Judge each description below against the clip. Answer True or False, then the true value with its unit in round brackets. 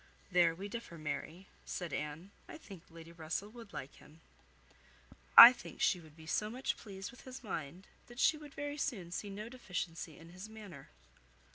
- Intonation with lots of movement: True (5.8 semitones)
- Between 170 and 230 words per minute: True (180 wpm)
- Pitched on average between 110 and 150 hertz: False (185 Hz)